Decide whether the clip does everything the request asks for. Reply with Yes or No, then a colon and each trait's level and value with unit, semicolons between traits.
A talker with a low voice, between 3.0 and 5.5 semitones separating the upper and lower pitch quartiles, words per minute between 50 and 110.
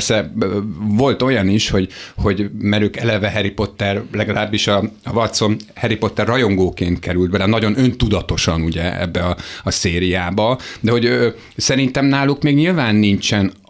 No: low, 105 Hz; average, 3.3 semitones; average, 140 wpm